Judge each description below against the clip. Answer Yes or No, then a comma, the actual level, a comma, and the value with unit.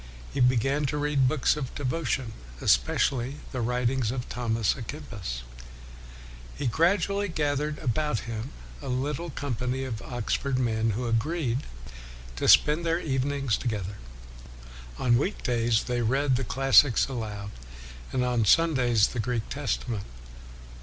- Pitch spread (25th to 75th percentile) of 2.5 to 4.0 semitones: Yes, average, 3.6 semitones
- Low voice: Yes, low, 125 Hz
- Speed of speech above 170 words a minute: No, slow, 135 wpm